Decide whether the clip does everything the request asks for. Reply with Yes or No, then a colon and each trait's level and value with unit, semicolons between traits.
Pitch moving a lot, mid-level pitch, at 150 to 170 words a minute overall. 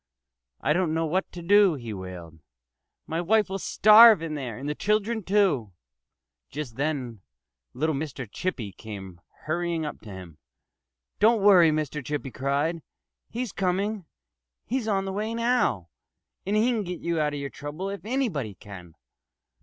Yes: wide, 7.6 semitones; medium, 160 Hz; average, 160 wpm